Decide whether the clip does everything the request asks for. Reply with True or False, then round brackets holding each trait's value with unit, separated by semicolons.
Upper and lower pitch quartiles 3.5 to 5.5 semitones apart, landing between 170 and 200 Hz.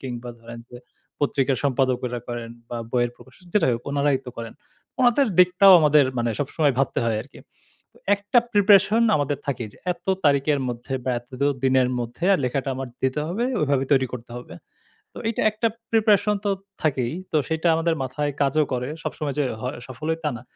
False (4.6 semitones; 140 Hz)